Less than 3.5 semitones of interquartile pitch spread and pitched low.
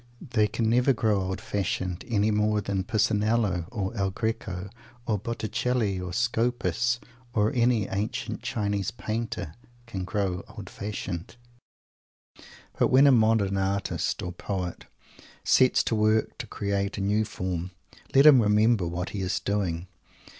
Yes: average, 3.0 semitones; low, 105 Hz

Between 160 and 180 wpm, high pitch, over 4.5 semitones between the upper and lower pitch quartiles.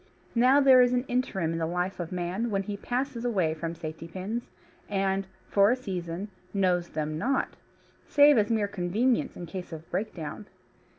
Yes: average, 175 wpm; high, 195 Hz; wide, 5.6 semitones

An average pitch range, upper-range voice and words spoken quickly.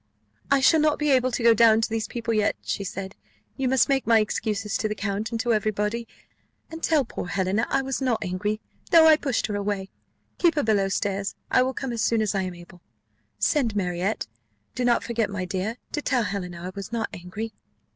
Yes: average, 4.1 semitones; high, 220 Hz; fast, 220 wpm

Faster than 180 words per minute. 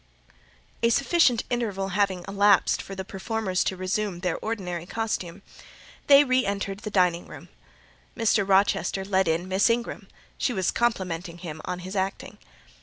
No: average, 150 wpm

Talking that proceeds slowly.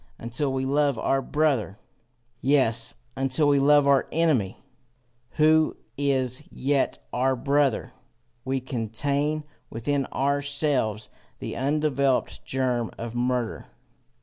Yes: slow, 105 wpm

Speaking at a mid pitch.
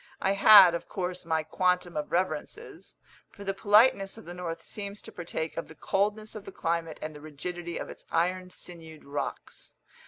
Yes: medium, 180 Hz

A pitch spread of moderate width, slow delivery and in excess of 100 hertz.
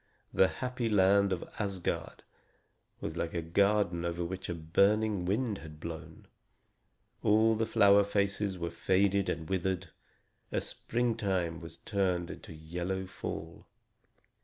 No: average, 3.1 semitones; slow, 130 wpm; very low, 95 Hz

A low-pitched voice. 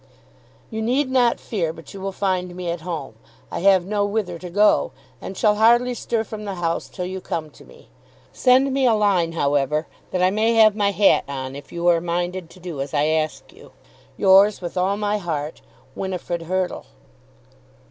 No: medium, 185 Hz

